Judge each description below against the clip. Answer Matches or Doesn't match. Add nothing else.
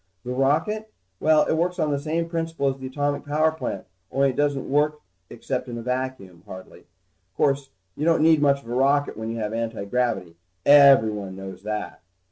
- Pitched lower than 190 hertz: Matches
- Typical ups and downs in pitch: Matches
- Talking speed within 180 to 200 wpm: Matches